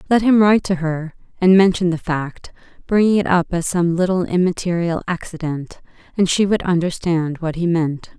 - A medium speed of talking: Yes, average, 175 wpm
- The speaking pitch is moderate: Yes, medium, 175 Hz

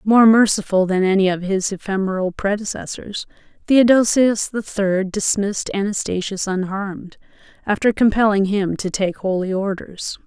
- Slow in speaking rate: Yes, slow, 125 wpm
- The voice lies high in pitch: Yes, high, 200 Hz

